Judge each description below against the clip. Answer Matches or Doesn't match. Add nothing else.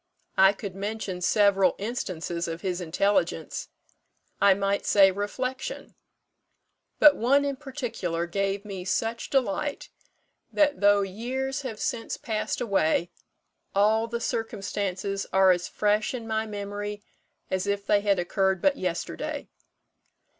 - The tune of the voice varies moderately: Matches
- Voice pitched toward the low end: Doesn't match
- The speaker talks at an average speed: Doesn't match